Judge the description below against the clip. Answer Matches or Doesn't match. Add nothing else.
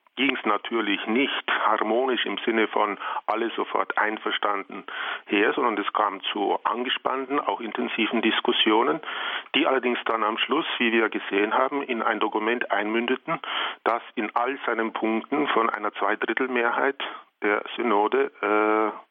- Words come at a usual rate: Matches